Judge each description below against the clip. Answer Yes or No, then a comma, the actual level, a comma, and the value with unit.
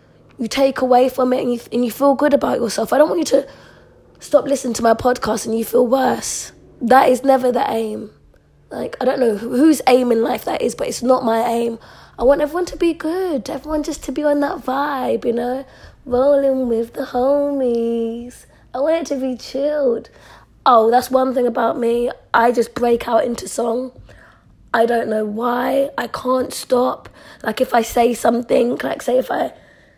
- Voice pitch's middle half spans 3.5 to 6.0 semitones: No, average, 2.8 semitones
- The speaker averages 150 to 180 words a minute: No, average, 200 wpm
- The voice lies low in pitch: No, very high, 250 Hz